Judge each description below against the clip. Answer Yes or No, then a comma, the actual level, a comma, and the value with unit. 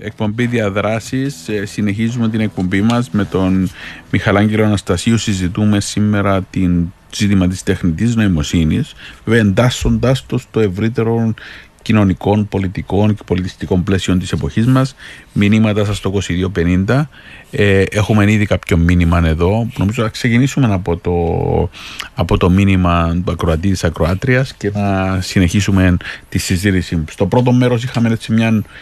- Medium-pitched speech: No, low, 100 Hz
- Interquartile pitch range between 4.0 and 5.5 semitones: No, average, 3.4 semitones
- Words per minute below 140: Yes, average, 130 wpm